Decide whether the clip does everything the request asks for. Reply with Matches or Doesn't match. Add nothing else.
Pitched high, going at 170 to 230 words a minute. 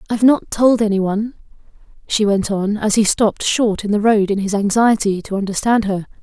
Matches